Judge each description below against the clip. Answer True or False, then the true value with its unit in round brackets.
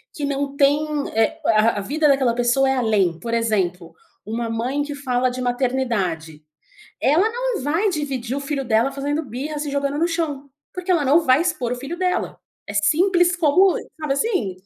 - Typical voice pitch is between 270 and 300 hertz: True (275 Hz)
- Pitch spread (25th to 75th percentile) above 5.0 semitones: False (4.6 semitones)